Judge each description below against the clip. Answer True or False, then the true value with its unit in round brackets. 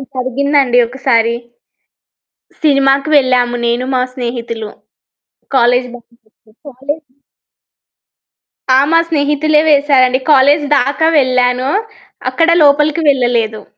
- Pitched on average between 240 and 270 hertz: True (260 Hz)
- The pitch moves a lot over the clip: False (2.8 semitones)